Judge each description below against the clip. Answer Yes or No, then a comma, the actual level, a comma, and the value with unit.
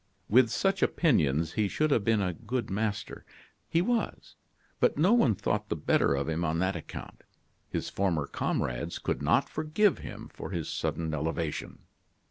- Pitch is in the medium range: No, low, 100 Hz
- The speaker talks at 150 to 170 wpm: Yes, average, 165 wpm